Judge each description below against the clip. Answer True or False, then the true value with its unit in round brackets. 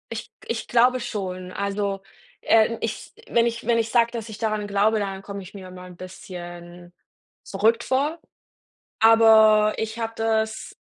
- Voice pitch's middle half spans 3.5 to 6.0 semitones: False (2.7 semitones)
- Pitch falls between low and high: False (215 Hz)